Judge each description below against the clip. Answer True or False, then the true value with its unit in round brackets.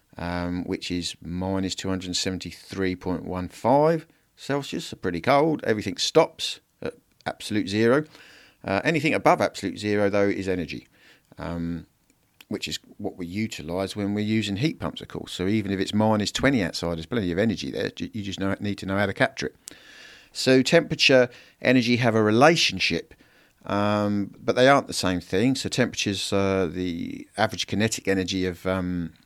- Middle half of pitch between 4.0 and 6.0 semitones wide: False (3.3 semitones)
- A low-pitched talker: True (95 Hz)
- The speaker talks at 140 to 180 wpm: True (160 wpm)